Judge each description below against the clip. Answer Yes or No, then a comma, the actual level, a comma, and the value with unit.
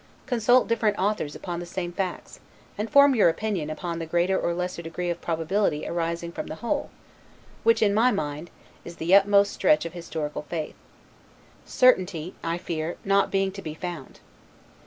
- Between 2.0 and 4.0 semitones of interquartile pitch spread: Yes, average, 3.4 semitones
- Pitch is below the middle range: No, medium, 175 Hz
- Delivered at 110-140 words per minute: No, average, 170 wpm